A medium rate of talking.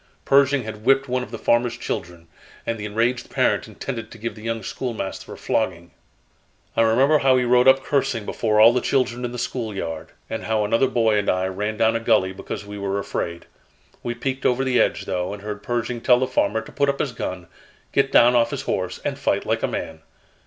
No: fast, 220 wpm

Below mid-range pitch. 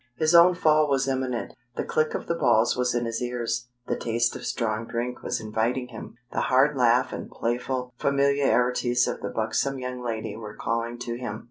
Yes: low, 125 Hz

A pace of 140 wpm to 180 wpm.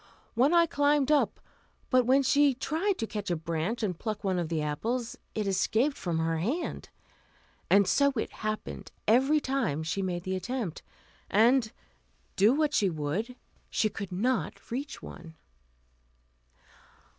Yes: average, 150 wpm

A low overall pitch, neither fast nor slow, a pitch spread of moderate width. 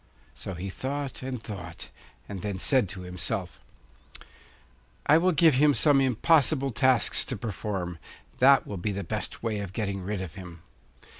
No: low, 105 Hz; average, 160 wpm; wide, 6.2 semitones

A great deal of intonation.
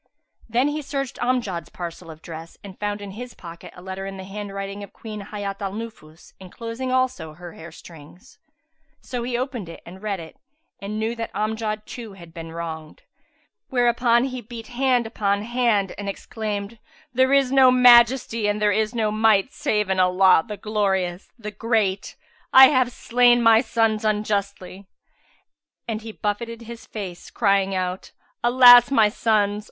No: average, 3.6 semitones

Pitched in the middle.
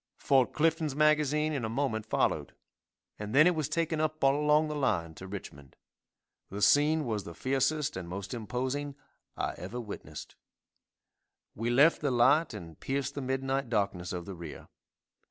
No: low, 130 Hz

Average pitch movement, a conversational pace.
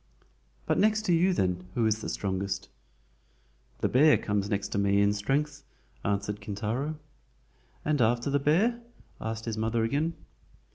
No: wide, 6.6 semitones; average, 150 wpm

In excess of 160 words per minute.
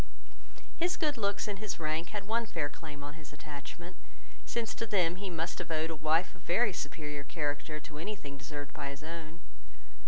Yes: average, 195 wpm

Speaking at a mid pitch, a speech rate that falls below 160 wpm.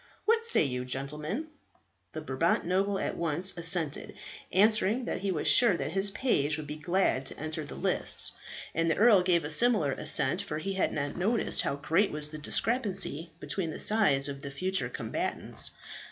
No: medium, 170 Hz; average, 180 wpm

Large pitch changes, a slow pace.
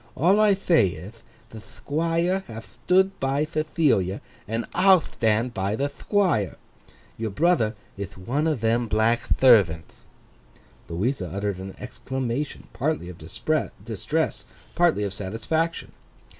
Yes: wide, 7.5 semitones; slow, 120 wpm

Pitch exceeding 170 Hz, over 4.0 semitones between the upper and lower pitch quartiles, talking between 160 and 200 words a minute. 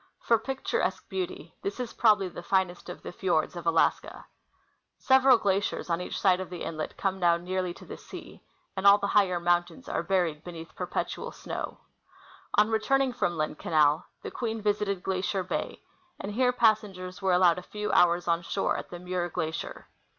No: medium, 185 Hz; average, 3.4 semitones; average, 180 wpm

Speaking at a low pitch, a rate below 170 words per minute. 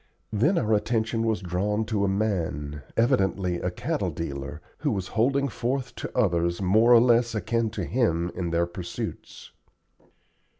Yes: low, 105 Hz; average, 155 wpm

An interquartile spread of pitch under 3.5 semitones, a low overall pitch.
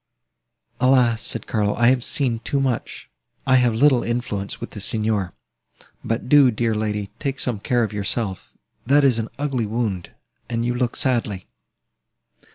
Yes: average, 3.1 semitones; low, 120 Hz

